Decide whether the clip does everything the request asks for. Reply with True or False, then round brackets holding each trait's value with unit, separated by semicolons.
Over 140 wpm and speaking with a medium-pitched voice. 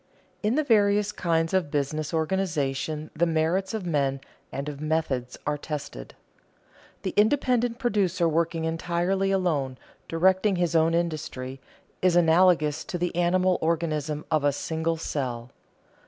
False (135 wpm; 165 Hz)